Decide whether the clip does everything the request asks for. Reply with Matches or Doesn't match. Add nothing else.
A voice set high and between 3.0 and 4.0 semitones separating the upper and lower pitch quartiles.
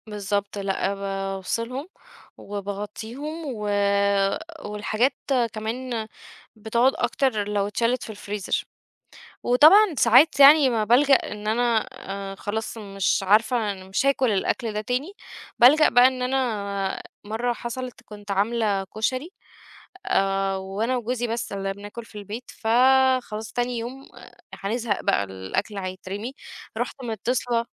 Matches